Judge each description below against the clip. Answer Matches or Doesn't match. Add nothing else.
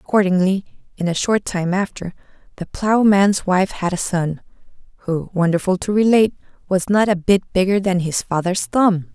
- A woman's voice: Matches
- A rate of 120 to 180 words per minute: Matches